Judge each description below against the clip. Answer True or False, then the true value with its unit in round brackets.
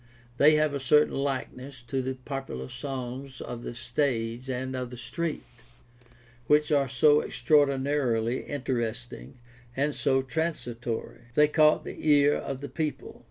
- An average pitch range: True (3.2 semitones)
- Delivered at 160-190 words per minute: False (140 wpm)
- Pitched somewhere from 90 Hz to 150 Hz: True (135 Hz)